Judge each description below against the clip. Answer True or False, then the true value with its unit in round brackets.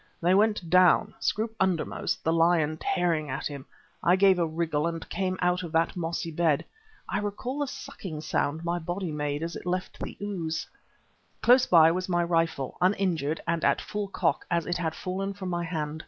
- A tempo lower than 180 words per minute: False (190 wpm)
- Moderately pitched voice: True (170 Hz)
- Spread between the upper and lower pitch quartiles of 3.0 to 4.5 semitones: False (2.5 semitones)